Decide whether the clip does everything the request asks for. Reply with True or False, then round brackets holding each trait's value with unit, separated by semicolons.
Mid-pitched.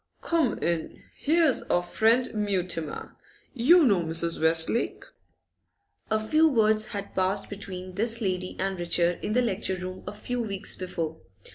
False (200 Hz)